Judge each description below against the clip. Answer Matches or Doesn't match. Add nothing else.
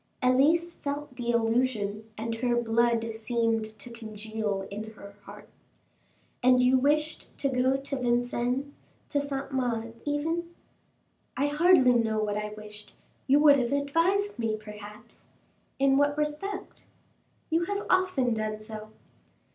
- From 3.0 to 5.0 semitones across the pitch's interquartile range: Matches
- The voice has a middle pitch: Doesn't match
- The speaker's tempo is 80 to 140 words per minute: Matches